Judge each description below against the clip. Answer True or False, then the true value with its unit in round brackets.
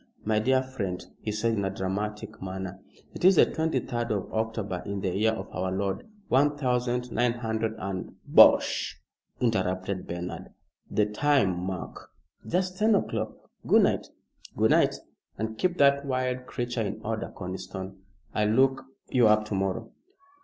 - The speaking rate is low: False (160 wpm)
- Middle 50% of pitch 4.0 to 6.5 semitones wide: True (4.8 semitones)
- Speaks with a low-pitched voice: True (110 Hz)